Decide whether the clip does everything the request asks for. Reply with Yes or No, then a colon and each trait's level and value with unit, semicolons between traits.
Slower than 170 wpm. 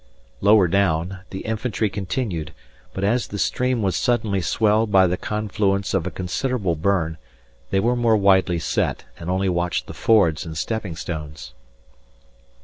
Yes: average, 150 wpm